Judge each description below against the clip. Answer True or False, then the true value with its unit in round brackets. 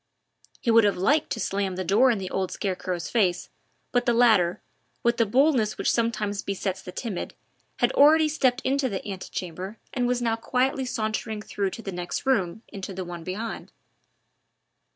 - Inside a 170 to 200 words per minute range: True (180 wpm)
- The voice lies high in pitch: True (215 Hz)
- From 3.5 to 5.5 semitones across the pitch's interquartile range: True (4.4 semitones)